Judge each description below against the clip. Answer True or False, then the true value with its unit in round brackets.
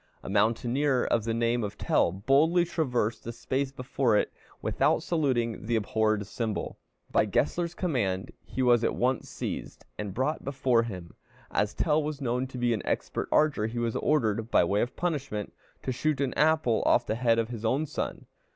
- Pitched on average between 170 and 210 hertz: False (120 Hz)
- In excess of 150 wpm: True (185 wpm)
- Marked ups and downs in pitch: False (3.9 semitones)